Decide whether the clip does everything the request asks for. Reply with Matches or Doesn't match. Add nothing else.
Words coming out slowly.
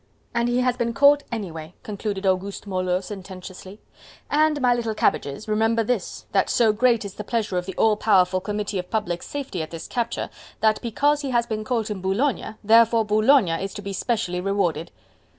Doesn't match